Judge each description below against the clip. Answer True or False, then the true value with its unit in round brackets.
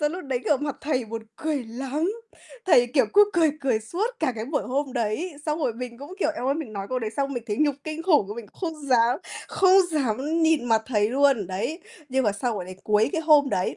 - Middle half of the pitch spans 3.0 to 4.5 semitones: False (5.1 semitones)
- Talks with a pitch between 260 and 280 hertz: True (270 Hz)